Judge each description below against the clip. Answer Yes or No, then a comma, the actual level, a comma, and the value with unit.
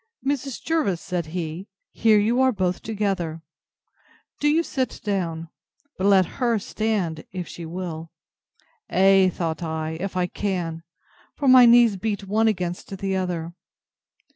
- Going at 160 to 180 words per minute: No, average, 140 wpm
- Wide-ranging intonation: No, average, 4.3 semitones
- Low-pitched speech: No, high, 190 Hz